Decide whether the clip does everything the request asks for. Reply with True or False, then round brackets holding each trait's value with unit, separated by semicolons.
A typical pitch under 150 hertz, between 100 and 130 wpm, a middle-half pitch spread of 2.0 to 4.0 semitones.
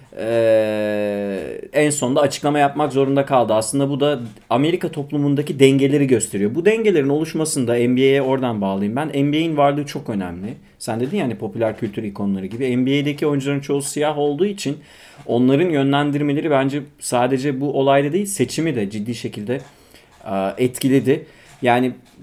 False (140 Hz; 140 wpm; 3.6 semitones)